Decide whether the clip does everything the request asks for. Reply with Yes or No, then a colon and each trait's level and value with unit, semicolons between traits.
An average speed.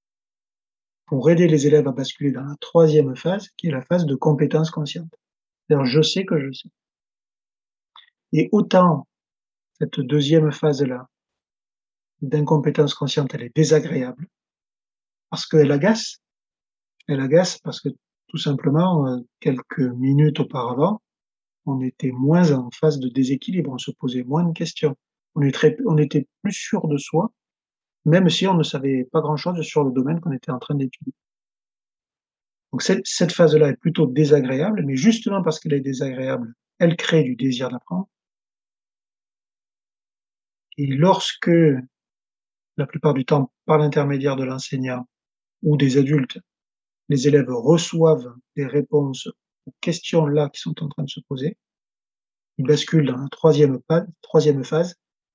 No: slow, 140 wpm